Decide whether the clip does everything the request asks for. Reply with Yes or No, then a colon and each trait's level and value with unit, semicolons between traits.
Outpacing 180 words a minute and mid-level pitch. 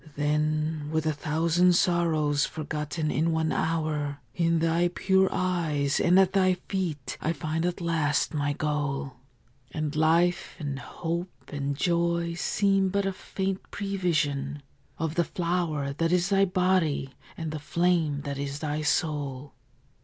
No: average, 145 wpm; medium, 160 Hz